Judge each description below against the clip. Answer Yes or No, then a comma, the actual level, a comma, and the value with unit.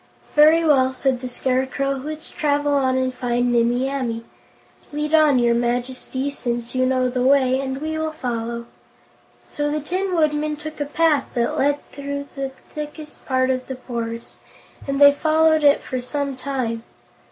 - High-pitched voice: Yes, very high, 270 Hz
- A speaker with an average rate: Yes, average, 165 wpm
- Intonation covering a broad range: No, average, 2.8 semitones